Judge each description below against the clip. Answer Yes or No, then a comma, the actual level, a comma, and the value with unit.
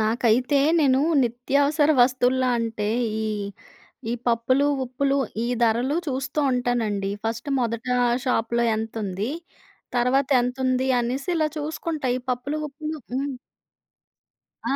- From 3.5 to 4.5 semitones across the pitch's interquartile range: No, average, 3.0 semitones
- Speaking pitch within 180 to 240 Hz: No, very high, 255 Hz